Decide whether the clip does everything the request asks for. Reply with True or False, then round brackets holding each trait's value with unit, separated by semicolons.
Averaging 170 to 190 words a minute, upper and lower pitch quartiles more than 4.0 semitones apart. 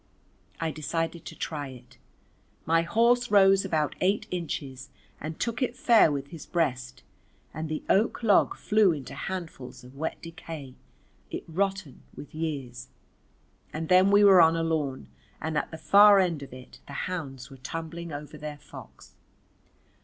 False (160 wpm; 4.8 semitones)